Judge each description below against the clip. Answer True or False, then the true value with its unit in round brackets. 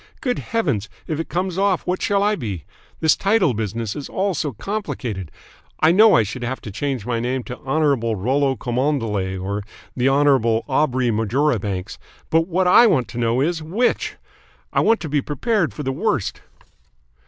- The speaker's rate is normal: True (175 wpm)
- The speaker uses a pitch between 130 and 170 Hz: True (135 Hz)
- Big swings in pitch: True (7.2 semitones)